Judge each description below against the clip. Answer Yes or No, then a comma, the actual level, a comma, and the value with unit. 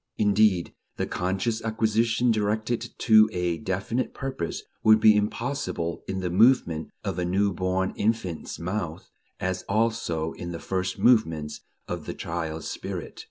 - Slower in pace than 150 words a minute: Yes, average, 140 wpm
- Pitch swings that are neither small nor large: Yes, average, 4.0 semitones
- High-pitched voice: No, very low, 95 Hz